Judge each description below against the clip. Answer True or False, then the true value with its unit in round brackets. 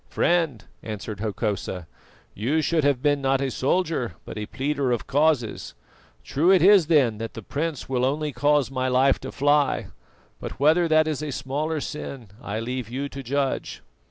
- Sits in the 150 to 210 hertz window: False (140 Hz)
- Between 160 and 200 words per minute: True (175 wpm)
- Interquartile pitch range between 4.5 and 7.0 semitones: False (3.5 semitones)